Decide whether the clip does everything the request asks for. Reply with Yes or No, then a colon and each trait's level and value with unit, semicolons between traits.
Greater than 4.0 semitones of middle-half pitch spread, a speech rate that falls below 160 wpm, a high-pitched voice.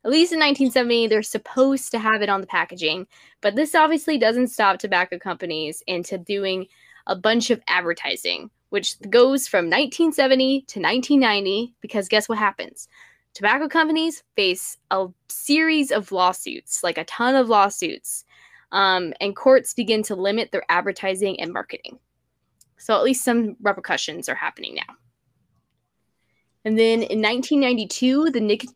Yes: average, 5.3 semitones; average, 150 wpm; high, 220 Hz